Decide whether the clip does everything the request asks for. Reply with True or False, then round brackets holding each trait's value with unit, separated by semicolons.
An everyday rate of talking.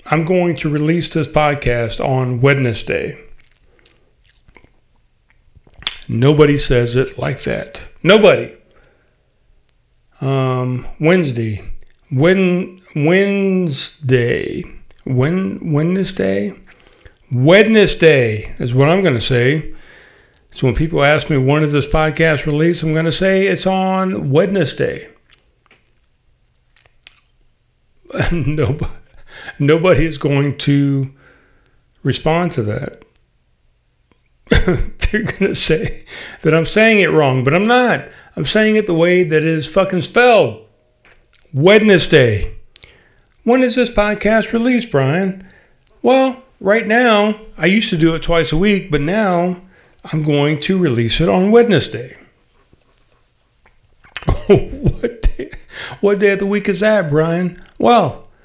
False (115 wpm)